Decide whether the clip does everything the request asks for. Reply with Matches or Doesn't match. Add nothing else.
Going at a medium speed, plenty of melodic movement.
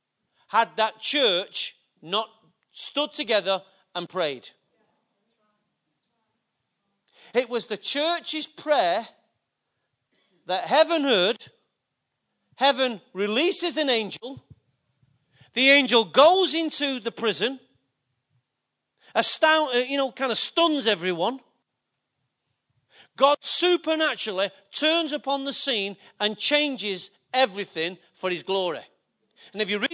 Doesn't match